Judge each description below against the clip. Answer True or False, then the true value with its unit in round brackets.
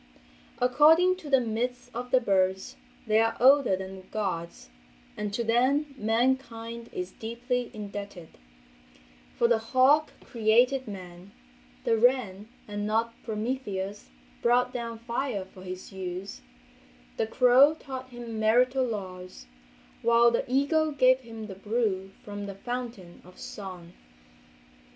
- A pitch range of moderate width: True (4.0 semitones)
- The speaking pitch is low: False (230 Hz)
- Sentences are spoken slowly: True (130 wpm)